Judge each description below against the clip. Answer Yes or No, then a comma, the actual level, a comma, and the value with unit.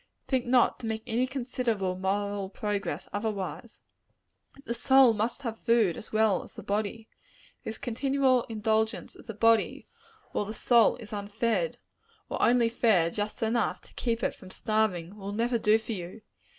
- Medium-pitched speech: No, high, 220 Hz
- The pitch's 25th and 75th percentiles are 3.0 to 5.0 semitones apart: No, narrow, 2.4 semitones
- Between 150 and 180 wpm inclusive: Yes, average, 165 wpm